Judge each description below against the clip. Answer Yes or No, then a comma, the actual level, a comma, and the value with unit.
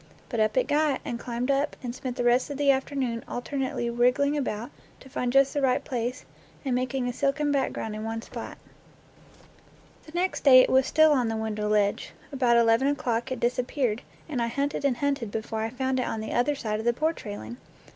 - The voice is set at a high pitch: Yes, very high, 250 Hz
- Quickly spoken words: Yes, fast, 210 wpm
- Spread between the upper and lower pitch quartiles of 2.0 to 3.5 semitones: Yes, average, 2.9 semitones